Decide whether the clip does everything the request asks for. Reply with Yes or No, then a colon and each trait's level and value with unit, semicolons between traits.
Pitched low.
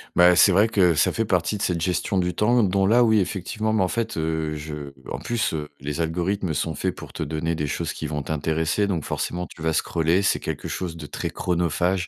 Yes: very low, 90 Hz